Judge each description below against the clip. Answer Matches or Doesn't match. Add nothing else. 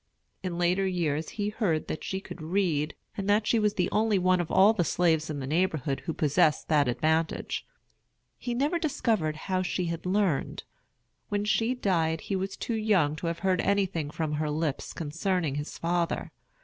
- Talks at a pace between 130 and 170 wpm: Doesn't match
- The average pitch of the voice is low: Doesn't match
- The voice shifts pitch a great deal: Doesn't match